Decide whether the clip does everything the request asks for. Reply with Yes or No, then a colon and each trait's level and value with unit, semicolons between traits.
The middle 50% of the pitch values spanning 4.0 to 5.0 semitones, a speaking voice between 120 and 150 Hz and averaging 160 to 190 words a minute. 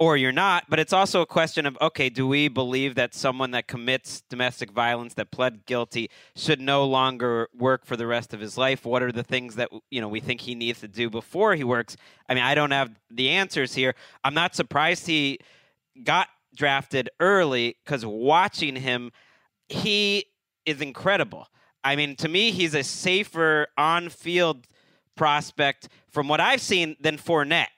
Yes: average, 4.4 semitones; low, 135 Hz; average, 180 wpm